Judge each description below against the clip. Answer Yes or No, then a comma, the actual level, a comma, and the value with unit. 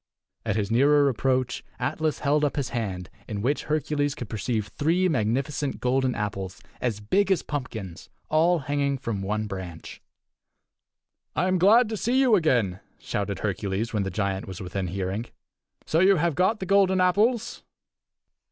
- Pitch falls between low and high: No, low, 130 Hz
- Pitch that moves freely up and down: Yes, wide, 8.2 semitones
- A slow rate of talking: No, average, 160 wpm